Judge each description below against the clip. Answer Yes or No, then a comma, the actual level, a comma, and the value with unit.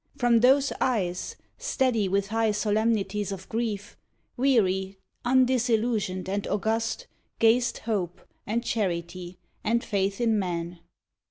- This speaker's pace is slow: Yes, slow, 110 wpm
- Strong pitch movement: No, average, 3.6 semitones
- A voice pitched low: No, high, 215 Hz